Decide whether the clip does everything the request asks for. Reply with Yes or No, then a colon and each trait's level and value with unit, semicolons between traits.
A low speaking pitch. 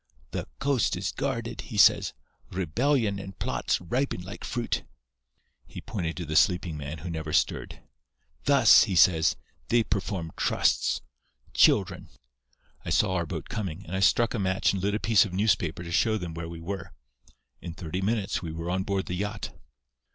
Yes: very low, 95 Hz